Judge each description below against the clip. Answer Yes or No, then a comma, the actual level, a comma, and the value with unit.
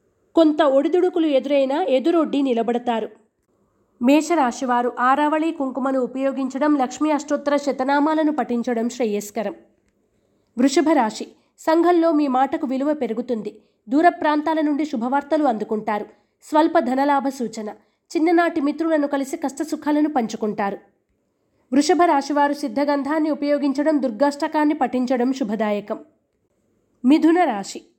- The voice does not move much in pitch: No, average, 3.8 semitones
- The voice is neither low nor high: No, very high, 280 Hz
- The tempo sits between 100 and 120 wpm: No, average, 90 wpm